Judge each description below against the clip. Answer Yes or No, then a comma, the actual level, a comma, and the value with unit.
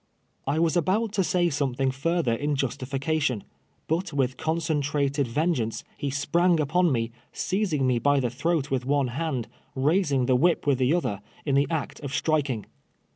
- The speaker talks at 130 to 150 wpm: No, average, 175 wpm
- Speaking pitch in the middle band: Yes, medium, 145 Hz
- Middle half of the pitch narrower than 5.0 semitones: Yes, average, 3.9 semitones